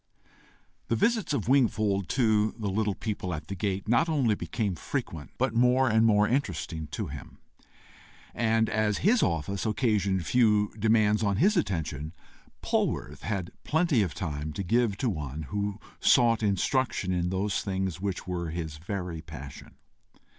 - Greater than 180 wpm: No, average, 155 wpm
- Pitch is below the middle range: Yes, low, 105 Hz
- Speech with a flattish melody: No, average, 4.2 semitones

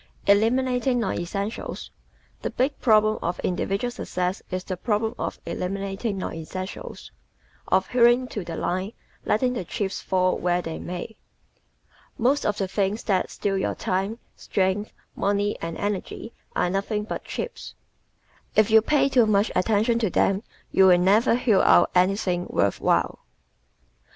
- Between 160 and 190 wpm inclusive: No, average, 150 wpm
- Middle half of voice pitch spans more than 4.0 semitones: No, average, 3.3 semitones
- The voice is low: No, high, 200 Hz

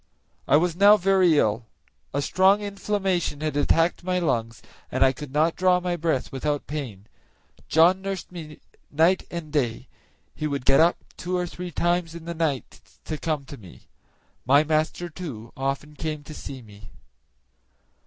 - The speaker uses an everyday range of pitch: Yes, average, 4.1 semitones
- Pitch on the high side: No, medium, 155 Hz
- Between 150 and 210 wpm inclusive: Yes, average, 165 wpm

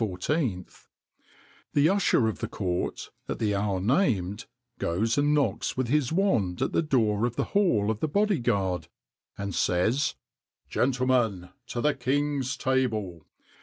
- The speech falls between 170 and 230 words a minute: No, average, 150 wpm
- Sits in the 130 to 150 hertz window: No, low, 120 Hz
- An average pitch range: No, wide, 6.2 semitones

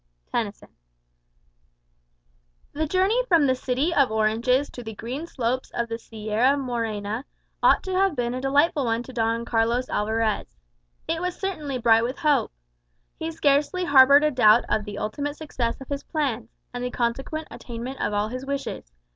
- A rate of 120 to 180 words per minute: Yes, average, 165 wpm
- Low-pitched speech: No, very high, 255 Hz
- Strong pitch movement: No, average, 4.2 semitones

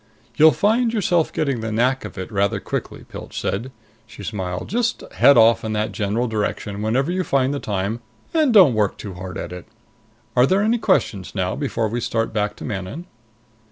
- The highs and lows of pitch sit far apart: Yes, wide, 7.0 semitones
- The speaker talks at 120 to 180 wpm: No, average, 190 wpm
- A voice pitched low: Yes, low, 115 Hz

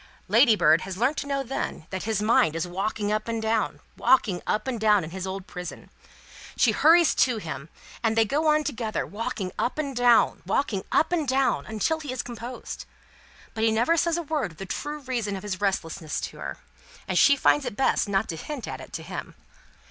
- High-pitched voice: Yes, high, 225 Hz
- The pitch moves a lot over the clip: Yes, wide, 5.7 semitones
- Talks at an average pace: No, fast, 210 wpm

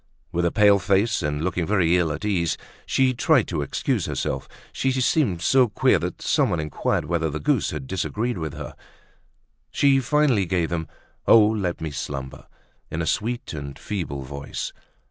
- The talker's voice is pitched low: Yes, very low, 90 Hz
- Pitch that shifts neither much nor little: No, wide, 6.0 semitones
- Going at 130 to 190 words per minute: Yes, average, 170 wpm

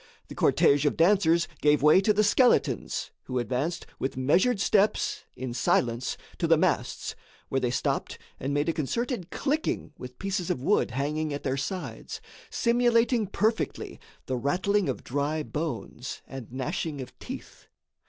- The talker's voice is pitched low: No, medium, 155 Hz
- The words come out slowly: No, average, 155 wpm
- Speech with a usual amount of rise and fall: No, wide, 7.2 semitones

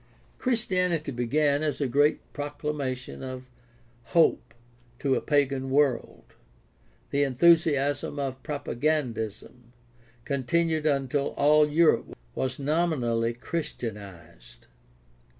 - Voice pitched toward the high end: No, medium, 140 Hz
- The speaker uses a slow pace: Yes, slow, 95 wpm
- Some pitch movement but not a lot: Yes, average, 3.2 semitones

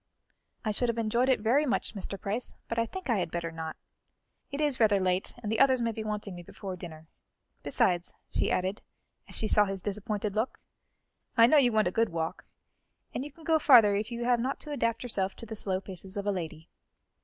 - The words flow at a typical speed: No, fast, 225 wpm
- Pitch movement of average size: Yes, average, 4.1 semitones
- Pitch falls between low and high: No, high, 215 Hz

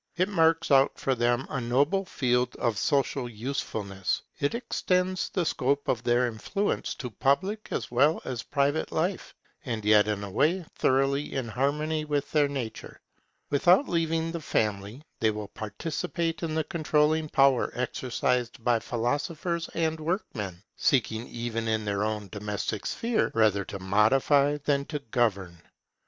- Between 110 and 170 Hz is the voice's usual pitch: Yes, low, 135 Hz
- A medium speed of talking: Yes, average, 150 wpm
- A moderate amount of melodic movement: No, wide, 6.0 semitones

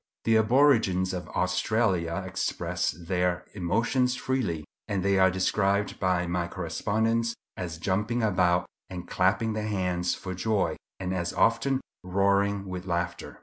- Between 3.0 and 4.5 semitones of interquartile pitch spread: Yes, average, 3.5 semitones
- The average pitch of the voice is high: No, very low, 95 Hz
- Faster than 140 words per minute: No, slow, 135 wpm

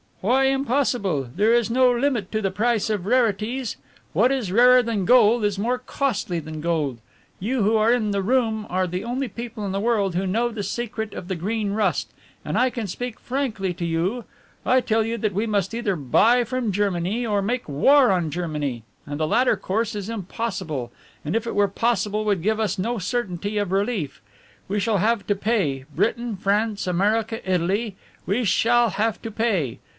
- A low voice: No, high, 215 Hz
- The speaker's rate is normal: Yes, average, 190 wpm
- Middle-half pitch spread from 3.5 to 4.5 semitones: Yes, average, 3.9 semitones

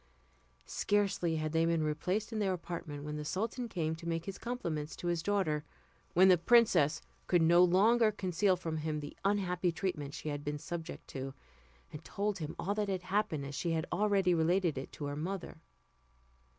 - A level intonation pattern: No, average, 4.1 semitones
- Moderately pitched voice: Yes, medium, 170 Hz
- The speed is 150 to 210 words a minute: Yes, average, 190 wpm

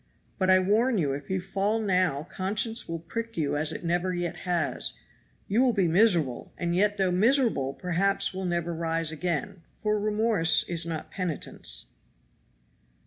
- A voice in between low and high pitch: Yes, medium, 180 Hz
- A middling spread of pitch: Yes, average, 3.9 semitones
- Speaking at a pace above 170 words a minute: No, average, 160 wpm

